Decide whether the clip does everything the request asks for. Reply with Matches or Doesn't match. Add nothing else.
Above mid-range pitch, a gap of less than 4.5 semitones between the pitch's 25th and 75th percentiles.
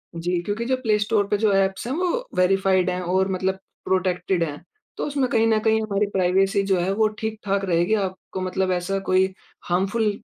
Matches